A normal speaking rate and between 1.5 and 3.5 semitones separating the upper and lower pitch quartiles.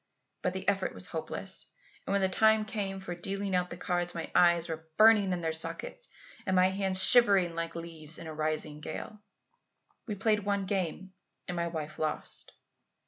Yes: average, 185 wpm; average, 3.1 semitones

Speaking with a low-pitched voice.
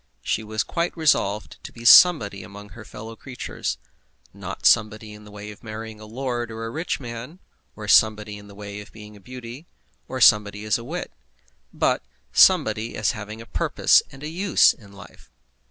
Yes: low, 110 Hz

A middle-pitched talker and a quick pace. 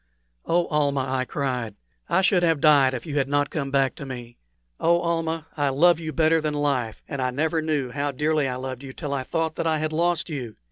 Yes: medium, 145 Hz; fast, 230 wpm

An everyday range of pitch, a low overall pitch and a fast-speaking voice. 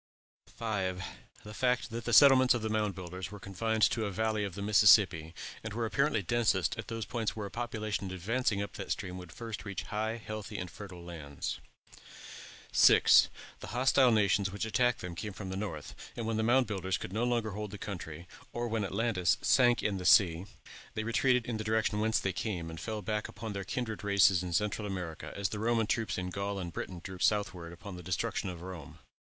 Yes: average, 3.3 semitones; low, 105 Hz; fast, 210 wpm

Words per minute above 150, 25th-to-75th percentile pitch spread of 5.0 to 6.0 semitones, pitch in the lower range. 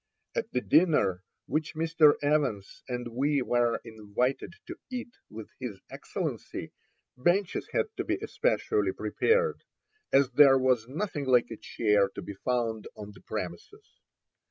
No: average, 140 wpm; wide, 5.6 semitones; low, 125 Hz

